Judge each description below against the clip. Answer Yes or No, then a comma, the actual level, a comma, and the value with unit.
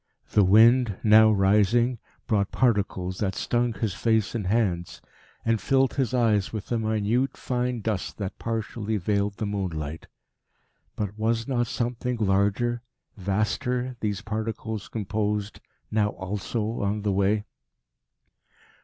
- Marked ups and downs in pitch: No, average, 2.7 semitones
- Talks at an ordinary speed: No, slow, 125 wpm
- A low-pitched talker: Yes, low, 110 Hz